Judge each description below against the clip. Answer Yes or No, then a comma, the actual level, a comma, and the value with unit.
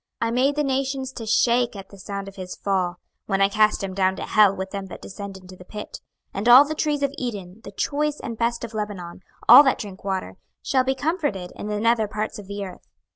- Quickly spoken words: Yes, fast, 240 wpm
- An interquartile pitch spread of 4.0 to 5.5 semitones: Yes, average, 4.6 semitones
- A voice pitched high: Yes, high, 210 Hz